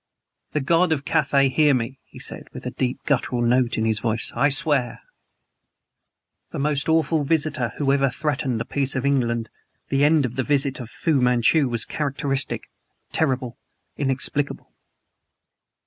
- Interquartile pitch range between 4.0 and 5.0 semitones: No, average, 2.8 semitones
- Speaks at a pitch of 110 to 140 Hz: Yes, low, 135 Hz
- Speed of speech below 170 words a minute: Yes, average, 160 wpm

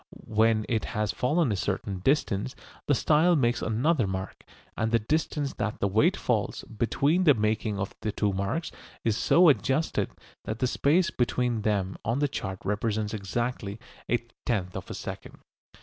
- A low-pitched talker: Yes, low, 110 Hz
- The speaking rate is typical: Yes, average, 165 wpm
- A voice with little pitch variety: No, average, 4.7 semitones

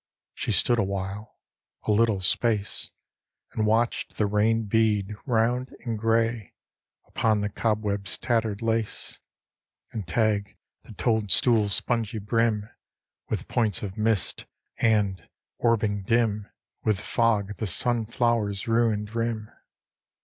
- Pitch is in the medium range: No, low, 110 Hz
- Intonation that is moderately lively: No, narrow, 2.0 semitones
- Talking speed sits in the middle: No, slow, 115 wpm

